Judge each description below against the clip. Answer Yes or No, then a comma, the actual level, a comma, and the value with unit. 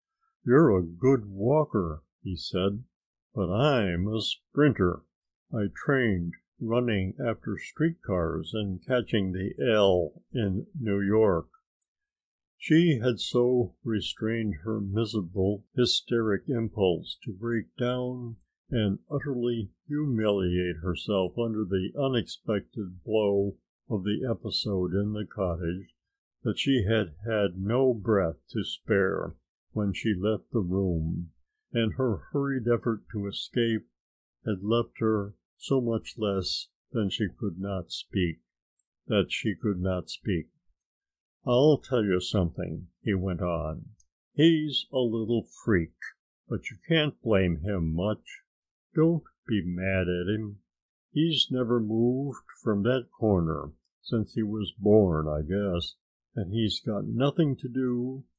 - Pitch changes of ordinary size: Yes, average, 4.6 semitones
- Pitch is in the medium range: No, low, 105 Hz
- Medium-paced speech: No, slow, 125 wpm